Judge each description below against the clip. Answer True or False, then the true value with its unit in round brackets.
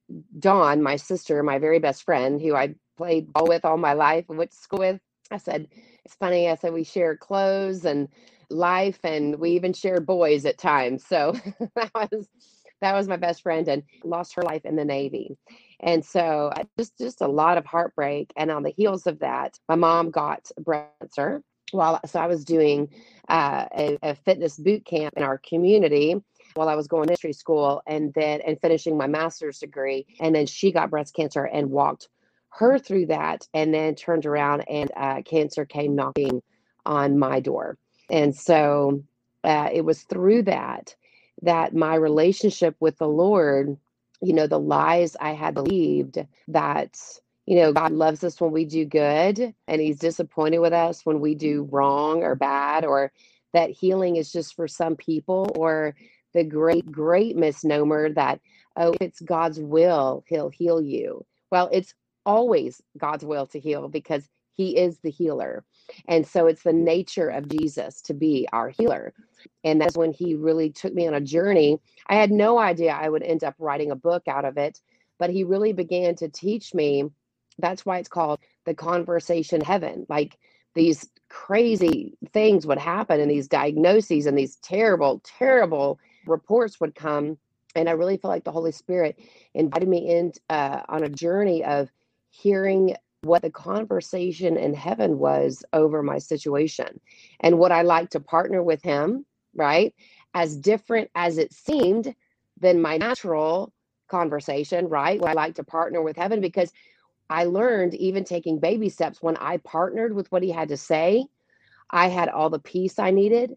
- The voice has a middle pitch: True (165 Hz)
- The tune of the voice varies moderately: True (3.2 semitones)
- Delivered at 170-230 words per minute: True (180 wpm)